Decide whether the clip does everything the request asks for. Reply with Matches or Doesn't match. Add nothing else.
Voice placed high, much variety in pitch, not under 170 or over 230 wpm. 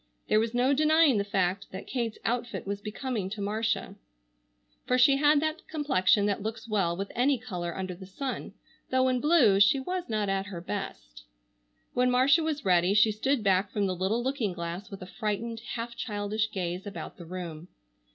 Doesn't match